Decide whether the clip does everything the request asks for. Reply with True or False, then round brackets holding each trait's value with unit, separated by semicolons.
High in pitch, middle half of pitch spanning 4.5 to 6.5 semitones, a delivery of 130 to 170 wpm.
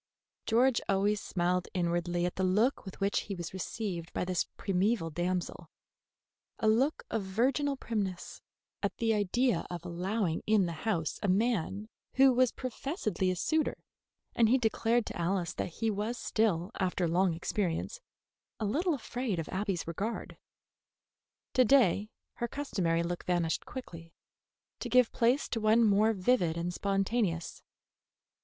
True (200 Hz; 4.8 semitones; 150 wpm)